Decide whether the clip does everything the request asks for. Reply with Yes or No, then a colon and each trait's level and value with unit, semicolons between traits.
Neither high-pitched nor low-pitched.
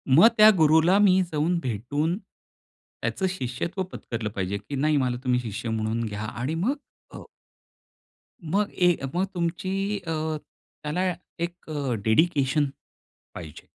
Yes: medium, 150 Hz